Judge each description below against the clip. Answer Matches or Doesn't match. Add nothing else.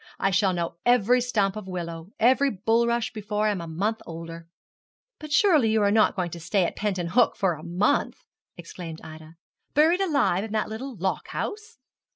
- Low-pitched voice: Doesn't match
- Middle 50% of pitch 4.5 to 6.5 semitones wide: Matches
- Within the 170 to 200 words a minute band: Matches